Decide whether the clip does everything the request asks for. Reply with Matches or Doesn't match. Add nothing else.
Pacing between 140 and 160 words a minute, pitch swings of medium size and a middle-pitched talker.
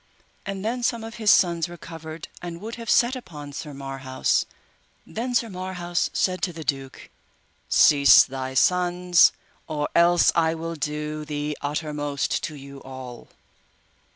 Matches